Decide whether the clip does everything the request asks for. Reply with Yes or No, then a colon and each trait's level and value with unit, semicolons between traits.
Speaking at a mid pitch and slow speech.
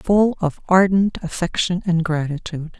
Yes: medium, 175 Hz; slow, 130 wpm